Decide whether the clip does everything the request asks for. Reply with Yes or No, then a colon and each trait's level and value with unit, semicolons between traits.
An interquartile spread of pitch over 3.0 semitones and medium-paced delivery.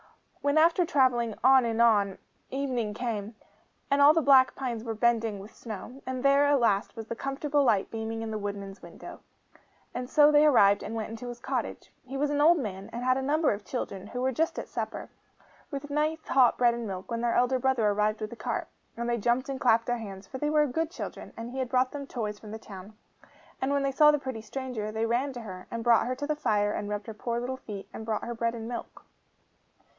No: average, 3.7 semitones; fast, 240 wpm